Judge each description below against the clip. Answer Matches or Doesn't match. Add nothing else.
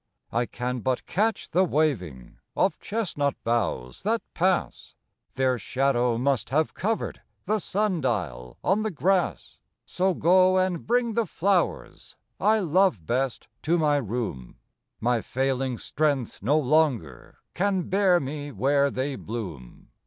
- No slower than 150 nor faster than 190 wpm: Doesn't match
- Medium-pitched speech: Matches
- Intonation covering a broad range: Matches